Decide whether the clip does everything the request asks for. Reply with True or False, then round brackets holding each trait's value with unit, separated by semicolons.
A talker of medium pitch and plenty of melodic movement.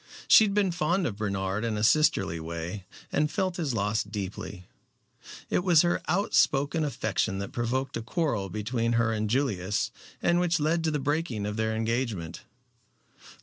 False (115 Hz; 7.3 semitones)